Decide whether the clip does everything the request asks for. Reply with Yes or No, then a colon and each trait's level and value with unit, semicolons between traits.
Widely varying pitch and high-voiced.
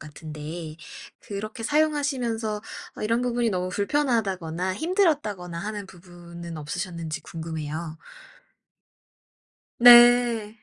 Yes: wide, 6.1 semitones; high, 200 Hz